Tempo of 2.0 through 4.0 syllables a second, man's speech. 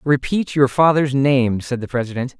No: 4.8 syllables/s; male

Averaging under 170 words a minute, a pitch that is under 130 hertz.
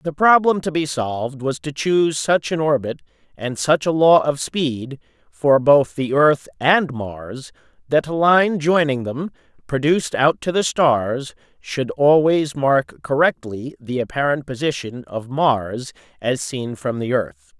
No: average, 160 wpm; medium, 140 Hz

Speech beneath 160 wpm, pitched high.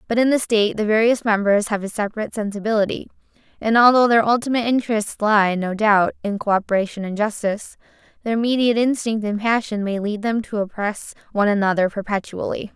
No: average, 170 wpm; high, 215 Hz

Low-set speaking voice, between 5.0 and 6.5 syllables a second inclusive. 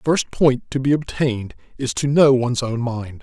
Yes: low, 125 Hz; 5.2 syllables/s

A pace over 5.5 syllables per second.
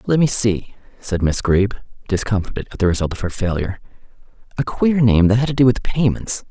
Yes: 5.8 syllables/s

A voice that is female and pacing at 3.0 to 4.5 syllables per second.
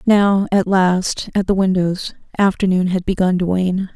Yes: female; 4.3 syllables/s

